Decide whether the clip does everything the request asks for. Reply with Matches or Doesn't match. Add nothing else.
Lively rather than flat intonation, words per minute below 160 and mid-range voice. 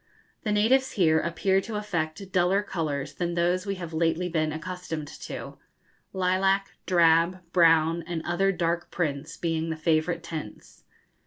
Doesn't match